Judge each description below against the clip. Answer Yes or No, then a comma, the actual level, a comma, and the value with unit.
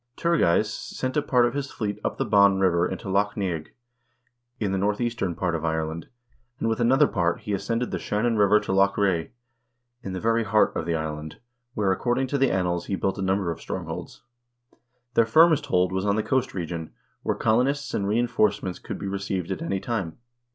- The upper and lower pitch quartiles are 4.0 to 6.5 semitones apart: Yes, average, 4.3 semitones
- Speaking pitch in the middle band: No, low, 100 Hz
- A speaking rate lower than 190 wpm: No, fast, 205 wpm